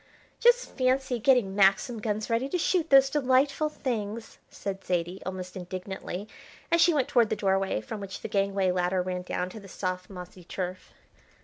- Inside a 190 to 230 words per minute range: No, average, 175 wpm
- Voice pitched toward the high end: Yes, high, 200 Hz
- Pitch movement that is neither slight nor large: No, wide, 5.7 semitones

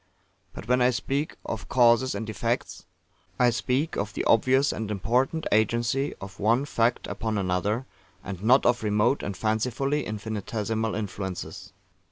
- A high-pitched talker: No, low, 115 Hz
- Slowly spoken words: No, average, 145 wpm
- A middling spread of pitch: Yes, average, 3.4 semitones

